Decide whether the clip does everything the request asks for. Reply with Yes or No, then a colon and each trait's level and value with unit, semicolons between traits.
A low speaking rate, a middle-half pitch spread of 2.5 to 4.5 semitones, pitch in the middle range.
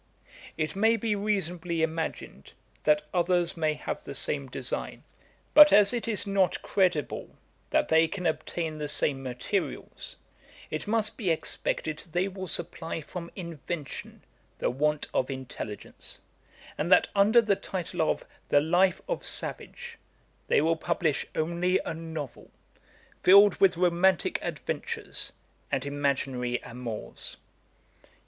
Yes: slow, 130 wpm; average, 4.1 semitones; medium, 165 Hz